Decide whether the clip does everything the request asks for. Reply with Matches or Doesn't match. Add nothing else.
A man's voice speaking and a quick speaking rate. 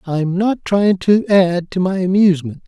Doesn't match